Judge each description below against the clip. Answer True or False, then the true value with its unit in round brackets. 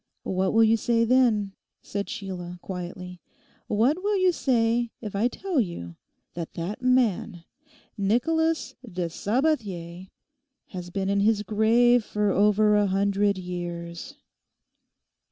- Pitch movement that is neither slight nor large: True (4.5 semitones)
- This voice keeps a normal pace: False (125 wpm)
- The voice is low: False (210 Hz)